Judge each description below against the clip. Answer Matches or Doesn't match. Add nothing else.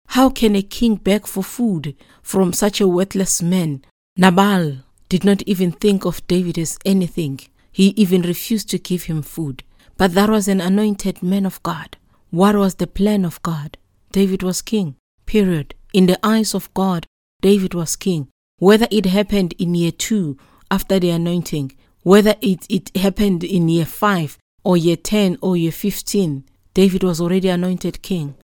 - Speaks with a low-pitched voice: Doesn't match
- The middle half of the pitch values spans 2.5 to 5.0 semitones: Matches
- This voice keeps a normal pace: Matches